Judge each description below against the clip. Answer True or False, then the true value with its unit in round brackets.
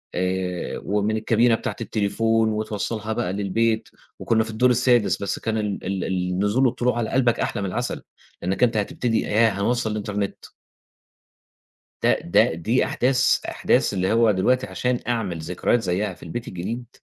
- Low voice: True (110 Hz)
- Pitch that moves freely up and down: False (3.3 semitones)